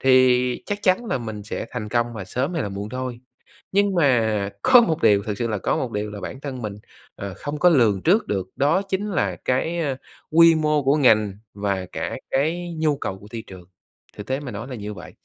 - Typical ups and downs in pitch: No, wide, 6.9 semitones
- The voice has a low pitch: Yes, low, 125 Hz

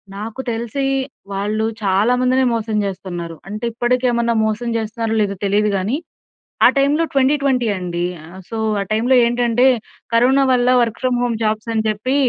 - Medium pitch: No, high, 230 Hz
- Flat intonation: No, average, 3.0 semitones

